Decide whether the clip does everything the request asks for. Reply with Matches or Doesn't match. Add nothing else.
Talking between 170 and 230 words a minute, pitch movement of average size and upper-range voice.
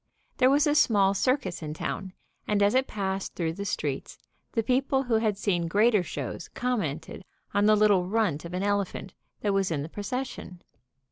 Matches